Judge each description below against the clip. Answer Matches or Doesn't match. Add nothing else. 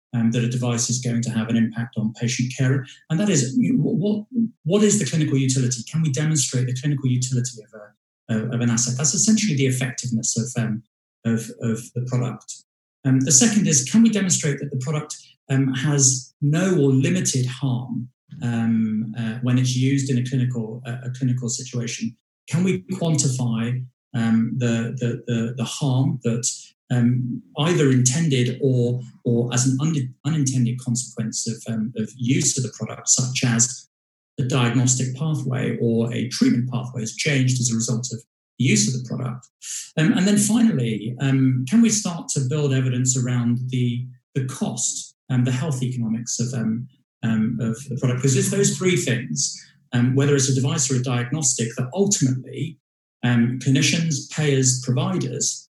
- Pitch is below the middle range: Matches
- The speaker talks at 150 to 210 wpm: Matches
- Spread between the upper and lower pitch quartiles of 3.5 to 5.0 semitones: Doesn't match